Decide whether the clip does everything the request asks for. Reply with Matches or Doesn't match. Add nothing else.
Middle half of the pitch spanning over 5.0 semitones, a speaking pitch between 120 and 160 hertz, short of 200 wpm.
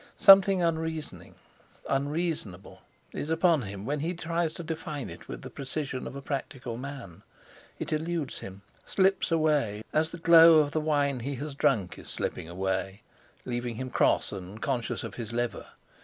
Matches